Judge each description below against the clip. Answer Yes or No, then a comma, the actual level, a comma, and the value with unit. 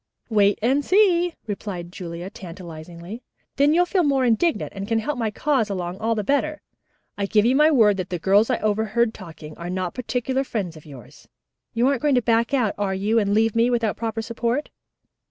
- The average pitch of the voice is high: Yes, high, 220 Hz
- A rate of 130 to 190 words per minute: No, average, 200 wpm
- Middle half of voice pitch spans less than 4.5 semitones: No, average, 5.1 semitones